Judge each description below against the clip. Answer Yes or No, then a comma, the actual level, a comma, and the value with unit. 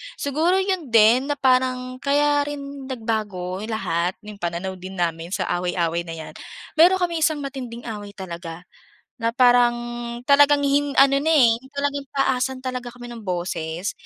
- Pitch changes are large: Yes, wide, 6.9 semitones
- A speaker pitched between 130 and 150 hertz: No, high, 245 Hz